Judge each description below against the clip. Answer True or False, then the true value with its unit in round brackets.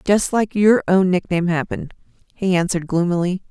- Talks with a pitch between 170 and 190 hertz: True (185 Hz)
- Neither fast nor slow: True (155 wpm)